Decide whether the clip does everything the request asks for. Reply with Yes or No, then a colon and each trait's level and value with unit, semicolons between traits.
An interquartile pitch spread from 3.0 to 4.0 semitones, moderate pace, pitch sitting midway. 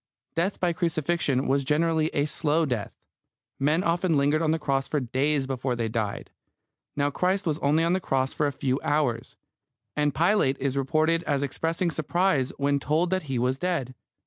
Yes: average, 3.6 semitones; average, 180 wpm; medium, 150 Hz